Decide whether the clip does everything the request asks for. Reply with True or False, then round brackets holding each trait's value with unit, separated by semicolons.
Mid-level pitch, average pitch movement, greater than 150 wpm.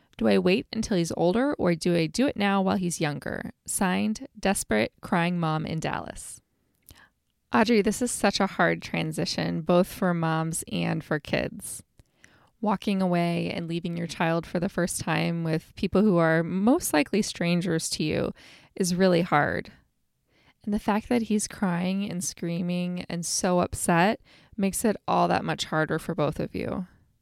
True (180 Hz; 3.2 semitones; 170 wpm)